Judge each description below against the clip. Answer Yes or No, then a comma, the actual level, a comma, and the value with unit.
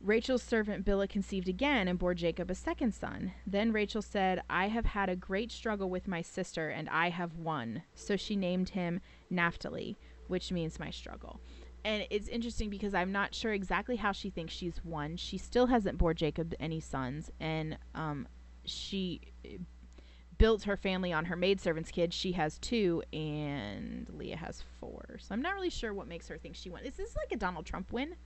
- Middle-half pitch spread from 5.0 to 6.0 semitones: No, average, 4.0 semitones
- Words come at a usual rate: Yes, average, 195 wpm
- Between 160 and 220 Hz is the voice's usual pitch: Yes, medium, 185 Hz